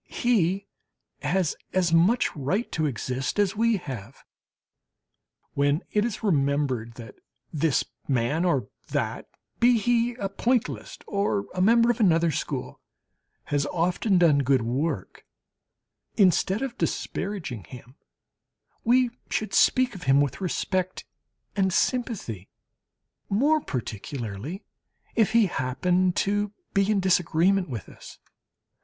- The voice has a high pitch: No, medium, 180 Hz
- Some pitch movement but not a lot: No, wide, 6.8 semitones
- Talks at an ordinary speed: No, slow, 120 wpm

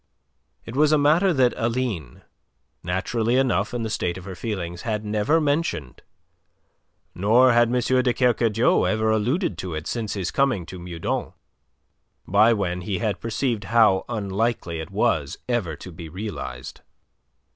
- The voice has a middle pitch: No, low, 110 Hz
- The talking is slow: No, average, 150 wpm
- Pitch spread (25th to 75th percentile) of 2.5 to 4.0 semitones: No, average, 5.2 semitones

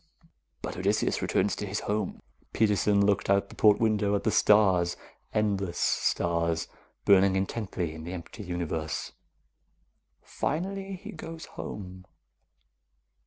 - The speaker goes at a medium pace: No, slow, 120 wpm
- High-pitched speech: No, low, 100 Hz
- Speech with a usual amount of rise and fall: Yes, average, 3.3 semitones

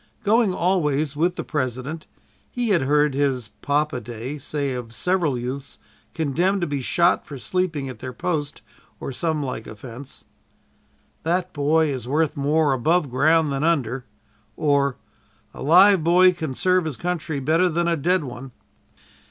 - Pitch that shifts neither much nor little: Yes, average, 4.3 semitones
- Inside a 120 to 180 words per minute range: Yes, average, 155 wpm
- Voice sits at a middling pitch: Yes, medium, 150 Hz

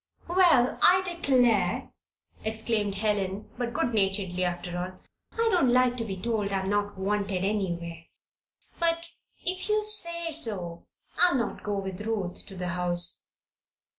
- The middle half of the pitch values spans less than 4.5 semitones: No, wide, 5.6 semitones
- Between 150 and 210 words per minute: No, average, 140 wpm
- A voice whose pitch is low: No, high, 210 Hz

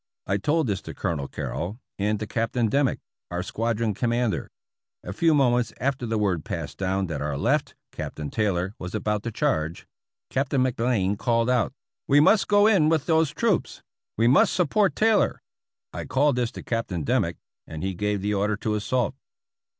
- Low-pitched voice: Yes, low, 115 Hz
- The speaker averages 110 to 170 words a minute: No, average, 185 wpm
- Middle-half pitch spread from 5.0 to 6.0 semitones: Yes, wide, 5.5 semitones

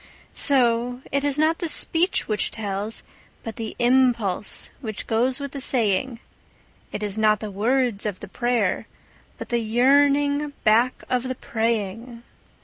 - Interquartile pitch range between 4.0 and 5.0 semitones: No, average, 3.5 semitones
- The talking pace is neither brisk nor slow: Yes, average, 150 wpm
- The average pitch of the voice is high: Yes, high, 240 Hz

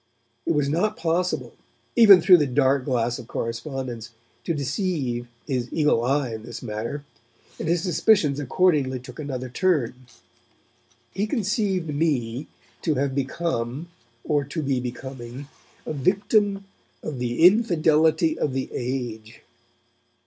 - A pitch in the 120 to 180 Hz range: Yes, medium, 140 Hz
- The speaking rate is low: Yes, slow, 130 wpm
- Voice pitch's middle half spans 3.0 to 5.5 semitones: Yes, average, 5.2 semitones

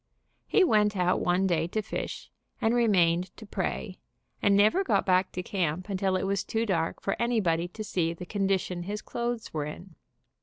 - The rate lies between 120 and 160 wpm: No, average, 185 wpm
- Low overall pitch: No, high, 190 Hz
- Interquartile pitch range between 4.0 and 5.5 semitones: No, average, 3.2 semitones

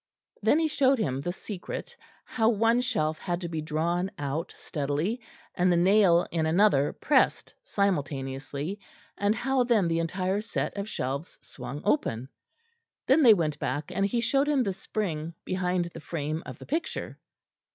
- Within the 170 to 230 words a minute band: No, average, 160 wpm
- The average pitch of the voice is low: No, medium, 180 Hz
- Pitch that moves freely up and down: Yes, wide, 6.1 semitones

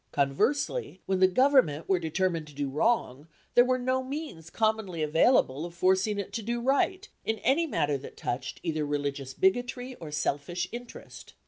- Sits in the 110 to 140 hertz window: No, medium, 185 Hz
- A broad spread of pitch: Yes, wide, 8.6 semitones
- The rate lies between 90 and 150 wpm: No, average, 165 wpm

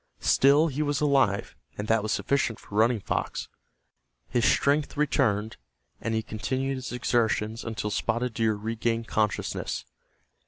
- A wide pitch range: No, average, 3.7 semitones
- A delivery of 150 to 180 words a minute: No, slow, 135 wpm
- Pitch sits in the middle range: No, low, 115 Hz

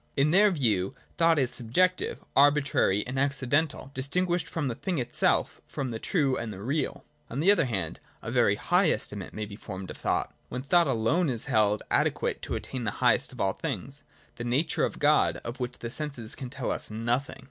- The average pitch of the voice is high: No, low, 130 Hz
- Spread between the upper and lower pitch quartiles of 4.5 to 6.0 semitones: Yes, average, 4.8 semitones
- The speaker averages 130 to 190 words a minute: No, average, 200 wpm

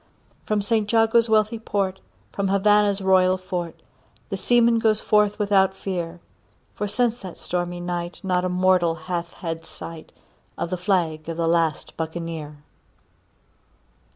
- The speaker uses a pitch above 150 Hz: Yes, medium, 185 Hz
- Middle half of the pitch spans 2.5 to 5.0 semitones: Yes, average, 3.4 semitones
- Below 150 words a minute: Yes, average, 140 wpm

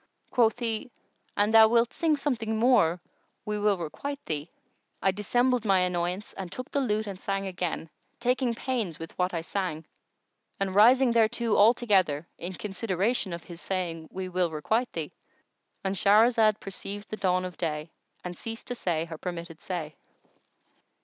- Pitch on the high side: Yes, high, 195 Hz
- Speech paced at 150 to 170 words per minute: Yes, average, 155 wpm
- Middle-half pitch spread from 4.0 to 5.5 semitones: Yes, average, 4.5 semitones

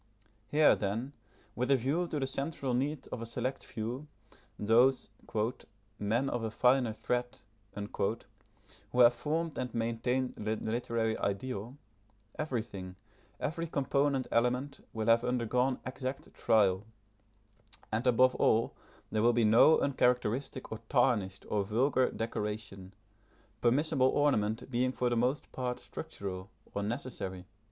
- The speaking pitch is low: Yes, low, 120 Hz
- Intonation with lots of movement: No, average, 3.2 semitones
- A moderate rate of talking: No, slow, 130 wpm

